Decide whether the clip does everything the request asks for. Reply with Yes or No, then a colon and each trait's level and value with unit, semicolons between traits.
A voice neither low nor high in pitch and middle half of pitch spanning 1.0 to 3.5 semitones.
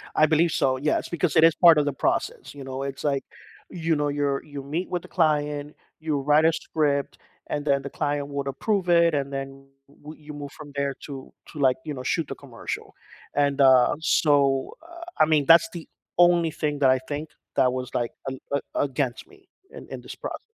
Yes: medium, 145 Hz; narrow, 2.5 semitones